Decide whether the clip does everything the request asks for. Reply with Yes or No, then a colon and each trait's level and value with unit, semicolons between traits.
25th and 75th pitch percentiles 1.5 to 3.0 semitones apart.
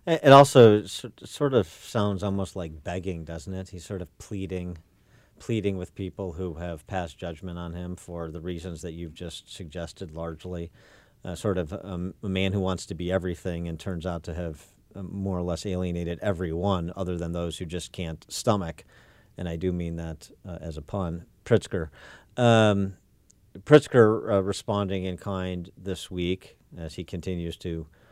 Yes: narrow, 2.4 semitones